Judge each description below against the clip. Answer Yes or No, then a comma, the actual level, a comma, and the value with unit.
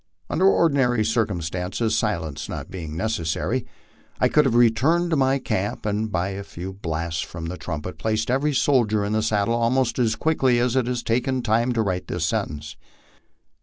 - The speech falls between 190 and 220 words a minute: No, average, 175 wpm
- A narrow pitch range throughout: No, wide, 5.5 semitones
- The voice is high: No, low, 110 Hz